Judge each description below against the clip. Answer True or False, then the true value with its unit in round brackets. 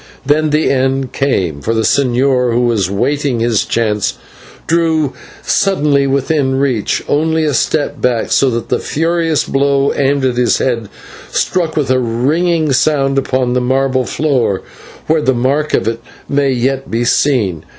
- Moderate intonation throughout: True (3.3 semitones)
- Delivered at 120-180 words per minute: True (160 wpm)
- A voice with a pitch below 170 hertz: True (135 Hz)